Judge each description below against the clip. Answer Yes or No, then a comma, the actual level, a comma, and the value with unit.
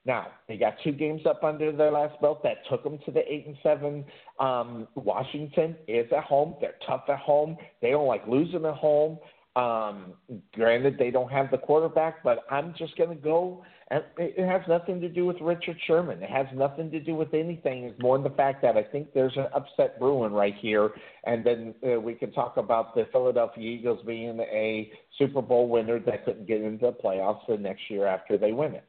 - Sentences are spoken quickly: Yes, fast, 215 wpm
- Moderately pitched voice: Yes, medium, 145 Hz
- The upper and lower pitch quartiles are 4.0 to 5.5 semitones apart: Yes, average, 5.1 semitones